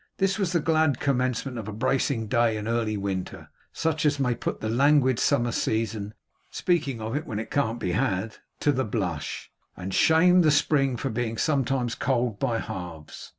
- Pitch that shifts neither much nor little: Yes, average, 4.7 semitones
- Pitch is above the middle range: No, low, 120 Hz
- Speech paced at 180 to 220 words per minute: Yes, average, 185 wpm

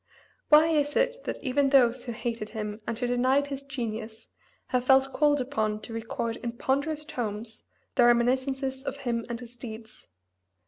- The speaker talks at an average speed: Yes, average, 170 wpm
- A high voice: Yes, very high, 250 Hz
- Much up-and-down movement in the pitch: No, average, 3.1 semitones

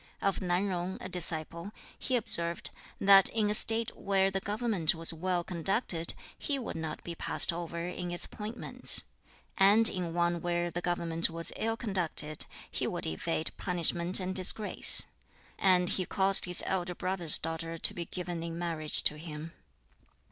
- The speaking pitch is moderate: Yes, medium, 175 Hz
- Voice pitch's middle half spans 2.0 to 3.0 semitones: Yes, narrow, 2.5 semitones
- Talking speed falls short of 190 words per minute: Yes, average, 160 wpm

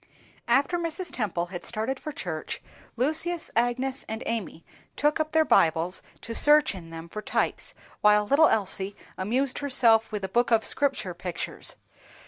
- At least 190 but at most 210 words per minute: No, average, 155 wpm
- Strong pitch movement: Yes, wide, 6.8 semitones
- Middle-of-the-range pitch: No, high, 230 Hz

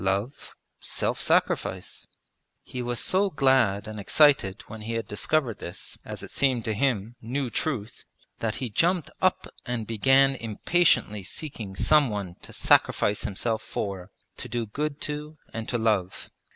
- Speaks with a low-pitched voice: Yes, low, 115 Hz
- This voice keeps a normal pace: Yes, average, 150 wpm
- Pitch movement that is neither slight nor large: Yes, average, 5.0 semitones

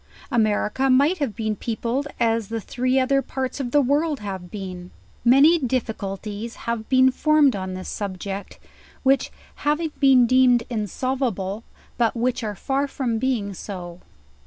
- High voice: Yes, high, 240 Hz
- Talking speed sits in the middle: Yes, average, 145 wpm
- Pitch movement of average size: Yes, average, 4.4 semitones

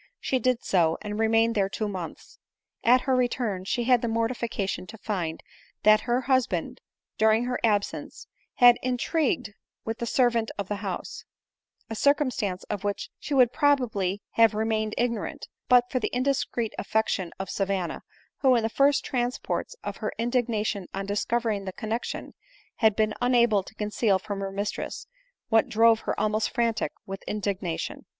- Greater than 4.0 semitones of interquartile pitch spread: No, average, 3.2 semitones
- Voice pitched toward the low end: No, high, 225 Hz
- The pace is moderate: Yes, average, 165 wpm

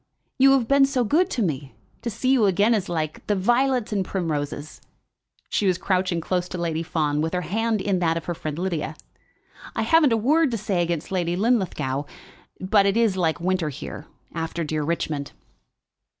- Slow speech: No, average, 190 wpm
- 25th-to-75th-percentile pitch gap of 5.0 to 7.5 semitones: Yes, wide, 5.5 semitones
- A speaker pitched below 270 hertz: Yes, medium, 185 Hz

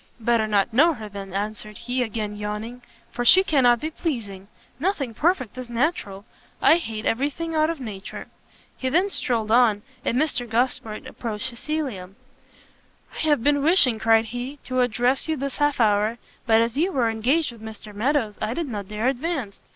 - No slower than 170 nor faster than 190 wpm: Yes, average, 180 wpm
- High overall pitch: Yes, high, 240 Hz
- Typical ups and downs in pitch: Yes, average, 5.0 semitones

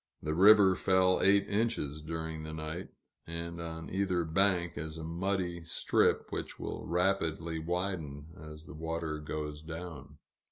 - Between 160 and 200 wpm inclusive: No, average, 145 wpm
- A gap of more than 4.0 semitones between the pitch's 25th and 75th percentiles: No, average, 2.9 semitones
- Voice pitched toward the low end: Yes, very low, 85 Hz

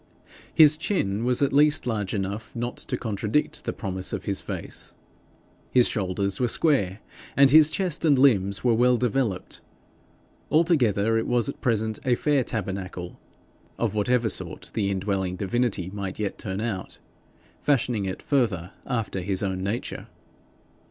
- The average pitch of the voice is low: Yes, low, 110 Hz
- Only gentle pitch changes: No, average, 4.3 semitones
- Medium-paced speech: Yes, average, 145 wpm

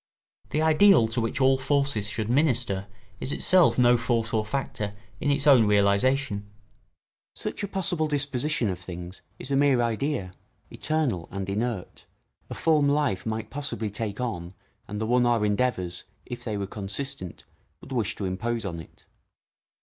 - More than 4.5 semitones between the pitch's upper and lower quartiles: Yes, wide, 5.5 semitones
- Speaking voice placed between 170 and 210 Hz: No, low, 120 Hz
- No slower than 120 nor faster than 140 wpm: No, average, 160 wpm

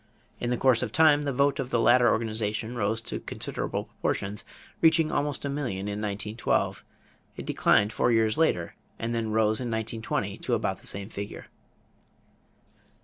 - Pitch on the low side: Yes, low, 115 Hz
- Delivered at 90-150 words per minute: No, average, 165 wpm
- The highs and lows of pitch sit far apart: No, average, 3.3 semitones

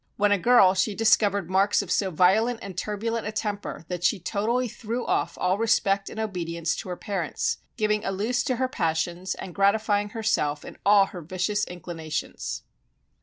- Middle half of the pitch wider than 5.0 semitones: No, average, 3.2 semitones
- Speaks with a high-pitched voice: Yes, high, 200 Hz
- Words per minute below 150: No, average, 175 wpm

